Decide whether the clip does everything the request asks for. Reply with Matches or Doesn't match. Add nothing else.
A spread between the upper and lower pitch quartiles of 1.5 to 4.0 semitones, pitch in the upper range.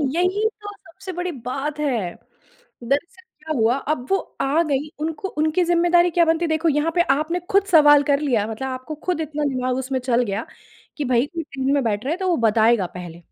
Doesn't match